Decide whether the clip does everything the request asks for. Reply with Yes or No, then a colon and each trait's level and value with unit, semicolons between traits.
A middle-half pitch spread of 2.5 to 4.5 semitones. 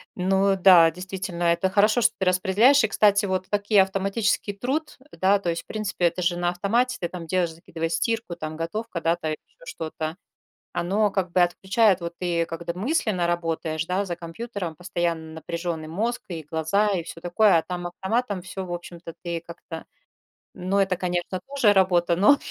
Yes: average, 3.0 semitones